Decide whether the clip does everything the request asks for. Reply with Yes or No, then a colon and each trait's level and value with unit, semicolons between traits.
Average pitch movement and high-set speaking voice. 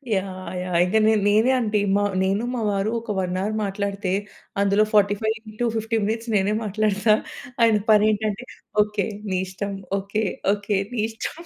No: narrow, 1.8 semitones; high, 210 Hz